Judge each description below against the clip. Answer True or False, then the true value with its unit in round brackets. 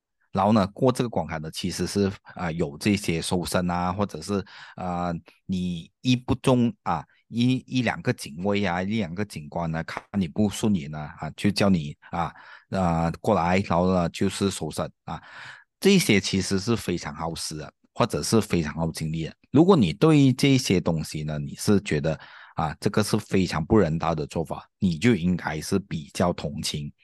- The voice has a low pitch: True (95 Hz)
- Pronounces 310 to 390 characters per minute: False (260 characters per minute)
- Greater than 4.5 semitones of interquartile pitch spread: True (5.5 semitones)